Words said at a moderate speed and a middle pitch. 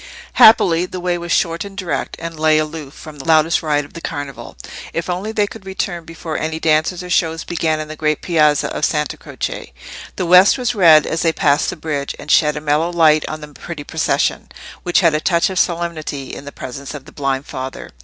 No: fast, 220 wpm; medium, 160 Hz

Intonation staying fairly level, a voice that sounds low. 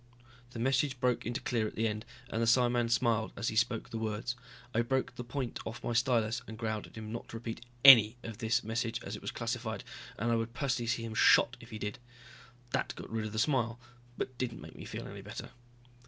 Yes: narrow, 1.5 semitones; low, 115 Hz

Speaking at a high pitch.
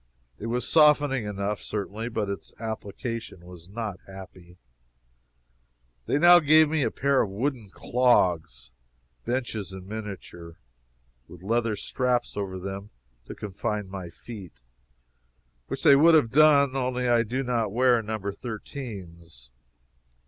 No: low, 110 Hz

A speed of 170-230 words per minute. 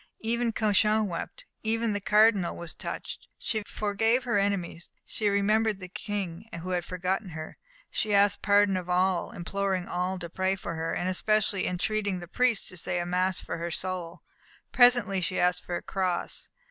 Yes: average, 175 wpm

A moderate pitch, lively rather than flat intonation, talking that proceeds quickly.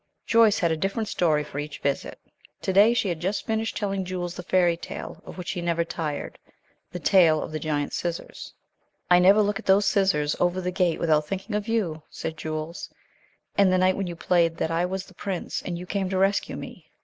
No: medium, 180 Hz; average, 2.9 semitones; fast, 220 wpm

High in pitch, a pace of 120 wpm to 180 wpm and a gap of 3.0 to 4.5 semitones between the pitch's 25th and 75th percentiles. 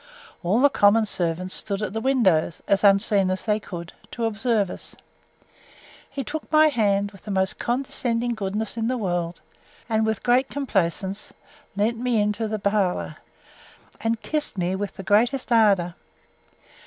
Yes: high, 210 Hz; average, 155 wpm; average, 3.5 semitones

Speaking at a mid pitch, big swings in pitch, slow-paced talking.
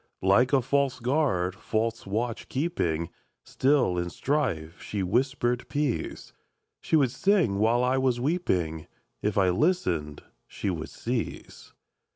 No: low, 120 Hz; wide, 6.6 semitones; slow, 130 wpm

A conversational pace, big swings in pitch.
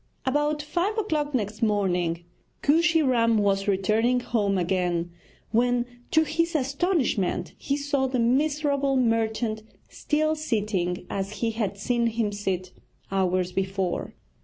No: slow, 125 wpm; wide, 6.5 semitones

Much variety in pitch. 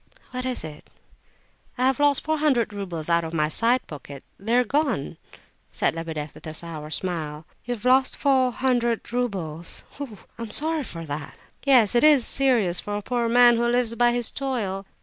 Yes: wide, 7.0 semitones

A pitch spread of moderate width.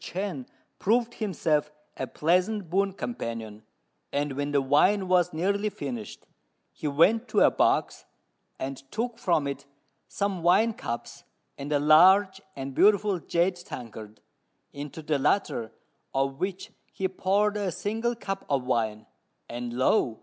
No: wide, 6.6 semitones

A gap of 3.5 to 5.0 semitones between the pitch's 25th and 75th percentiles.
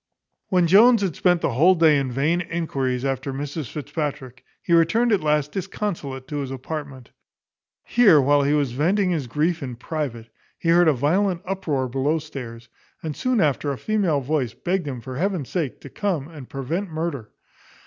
Yes: average, 4.5 semitones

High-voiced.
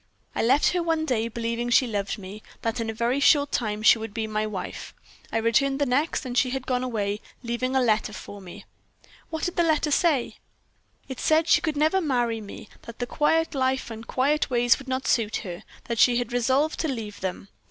Yes: high, 245 Hz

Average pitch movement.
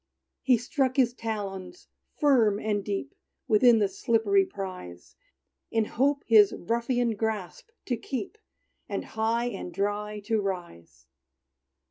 Yes: average, 3.3 semitones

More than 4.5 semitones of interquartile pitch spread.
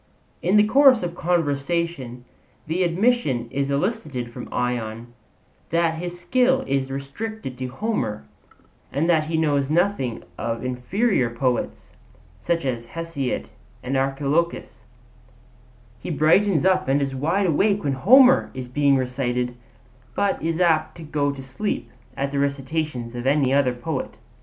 Yes: average, 5.1 semitones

